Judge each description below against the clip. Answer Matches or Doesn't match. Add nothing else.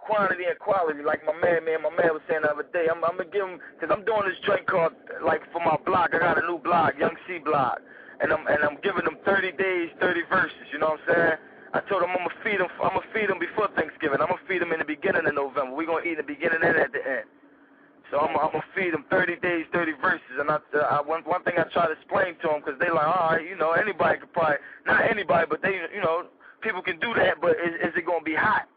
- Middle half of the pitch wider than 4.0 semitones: Doesn't match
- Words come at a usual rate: Doesn't match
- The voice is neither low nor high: Matches